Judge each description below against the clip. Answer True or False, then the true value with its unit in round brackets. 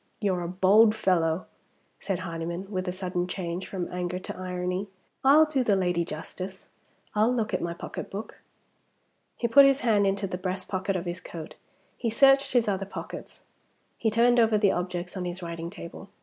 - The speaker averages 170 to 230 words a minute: True (180 wpm)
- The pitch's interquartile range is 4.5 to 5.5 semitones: False (3.3 semitones)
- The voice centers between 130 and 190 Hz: True (185 Hz)